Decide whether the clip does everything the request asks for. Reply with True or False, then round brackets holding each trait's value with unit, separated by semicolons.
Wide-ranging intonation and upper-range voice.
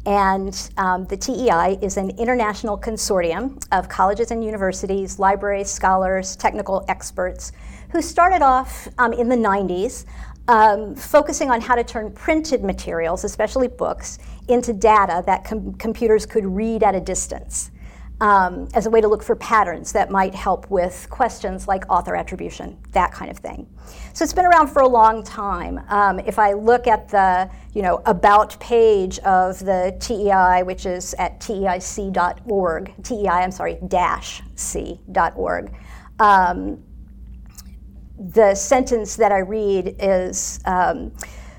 False (3.5 semitones; 200 Hz)